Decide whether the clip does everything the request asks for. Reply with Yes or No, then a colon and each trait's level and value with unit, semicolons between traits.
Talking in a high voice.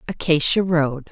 No: medium, 160 Hz